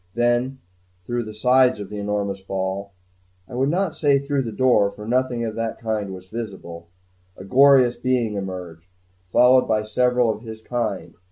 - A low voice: Yes, low, 115 Hz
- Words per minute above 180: No, average, 170 wpm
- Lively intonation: No, average, 4.0 semitones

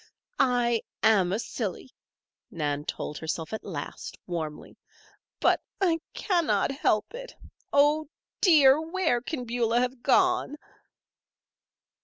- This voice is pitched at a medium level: No, high, 245 Hz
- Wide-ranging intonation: Yes, wide, 7.7 semitones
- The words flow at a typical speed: No, slow, 110 wpm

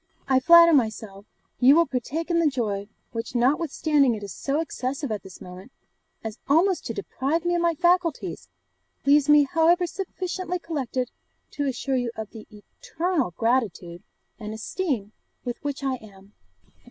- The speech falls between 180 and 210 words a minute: No, average, 160 wpm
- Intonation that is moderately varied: No, wide, 7.1 semitones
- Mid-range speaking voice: No, very high, 270 Hz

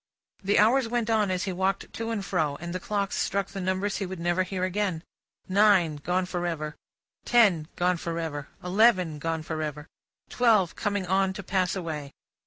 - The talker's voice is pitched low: No, medium, 185 Hz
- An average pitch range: Yes, average, 3.3 semitones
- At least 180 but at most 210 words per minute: Yes, average, 190 wpm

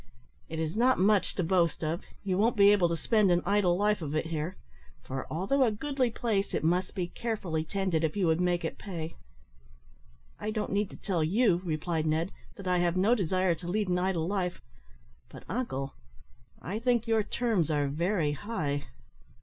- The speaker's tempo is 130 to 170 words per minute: No, average, 190 wpm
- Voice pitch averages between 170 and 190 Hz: Yes, medium, 185 Hz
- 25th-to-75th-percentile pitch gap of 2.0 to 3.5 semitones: No, average, 4.2 semitones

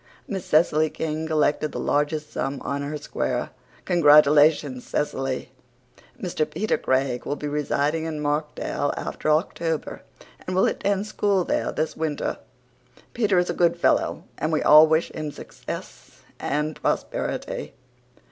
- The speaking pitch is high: No, medium, 155 Hz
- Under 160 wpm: Yes, average, 140 wpm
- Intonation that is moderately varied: No, narrow, 1.9 semitones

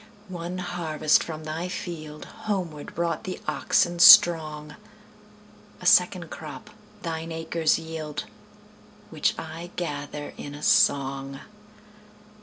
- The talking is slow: Yes, slow, 90 wpm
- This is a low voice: No, medium, 160 Hz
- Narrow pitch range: Yes, narrow, 2.3 semitones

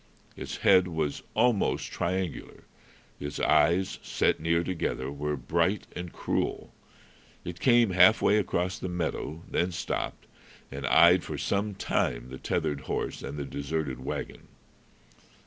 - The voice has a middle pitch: No, very low, 85 Hz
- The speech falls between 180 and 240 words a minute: No, slow, 135 wpm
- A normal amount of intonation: Yes, average, 4.3 semitones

